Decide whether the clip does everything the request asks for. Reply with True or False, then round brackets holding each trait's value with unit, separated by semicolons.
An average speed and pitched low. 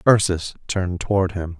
True (150 wpm; 90 Hz)